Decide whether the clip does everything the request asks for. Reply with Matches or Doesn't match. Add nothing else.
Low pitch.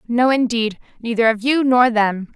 Doesn't match